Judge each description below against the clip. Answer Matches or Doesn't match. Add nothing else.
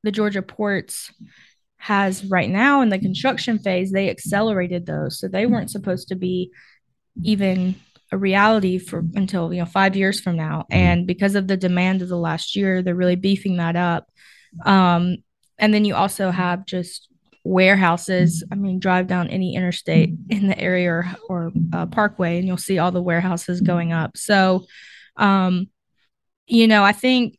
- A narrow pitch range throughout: Matches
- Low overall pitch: Doesn't match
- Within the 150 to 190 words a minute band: Matches